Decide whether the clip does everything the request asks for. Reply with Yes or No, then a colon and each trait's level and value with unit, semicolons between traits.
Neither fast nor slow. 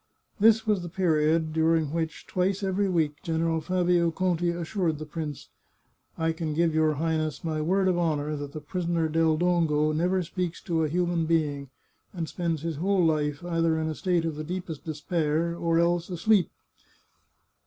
Yes: average, 175 wpm